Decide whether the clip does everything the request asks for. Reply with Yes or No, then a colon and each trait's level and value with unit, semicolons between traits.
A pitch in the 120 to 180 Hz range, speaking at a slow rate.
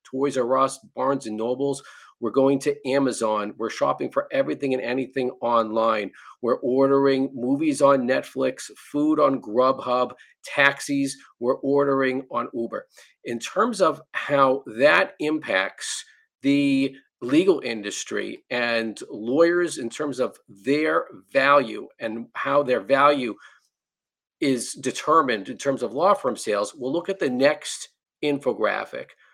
Yes: low, 135 Hz; slow, 130 wpm